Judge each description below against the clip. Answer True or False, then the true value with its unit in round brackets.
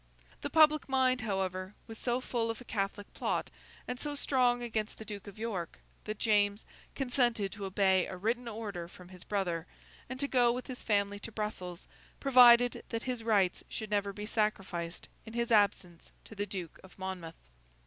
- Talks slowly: False (180 wpm)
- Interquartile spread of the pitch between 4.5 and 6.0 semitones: False (3.9 semitones)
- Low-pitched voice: False (210 Hz)